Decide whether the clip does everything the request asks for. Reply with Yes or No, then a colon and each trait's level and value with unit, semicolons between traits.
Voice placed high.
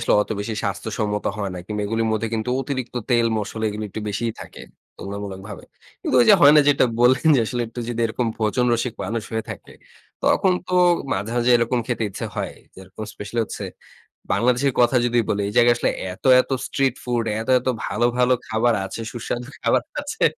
No: low, 115 Hz